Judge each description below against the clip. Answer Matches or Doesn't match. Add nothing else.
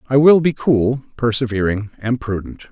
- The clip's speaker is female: Doesn't match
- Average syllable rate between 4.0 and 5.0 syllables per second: Matches